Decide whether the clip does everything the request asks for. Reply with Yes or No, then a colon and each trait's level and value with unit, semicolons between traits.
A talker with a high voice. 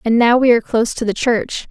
Yes: high, 230 Hz